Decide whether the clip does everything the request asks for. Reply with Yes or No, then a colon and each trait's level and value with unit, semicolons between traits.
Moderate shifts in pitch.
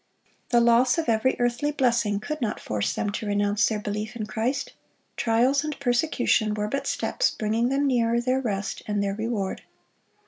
Yes: average, 3.3 semitones